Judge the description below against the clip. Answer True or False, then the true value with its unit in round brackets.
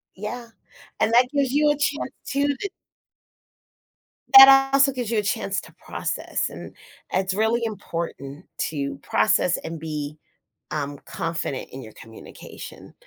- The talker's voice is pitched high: True (205 Hz)